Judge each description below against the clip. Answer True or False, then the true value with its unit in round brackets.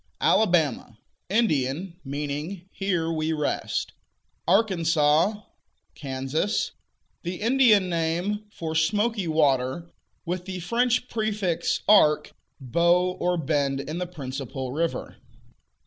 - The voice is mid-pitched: True (170 Hz)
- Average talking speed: False (100 wpm)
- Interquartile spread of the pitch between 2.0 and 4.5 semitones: False (4.9 semitones)